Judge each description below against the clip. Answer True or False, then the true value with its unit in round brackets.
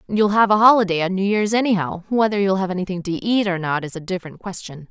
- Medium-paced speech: False (245 wpm)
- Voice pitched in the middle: False (195 Hz)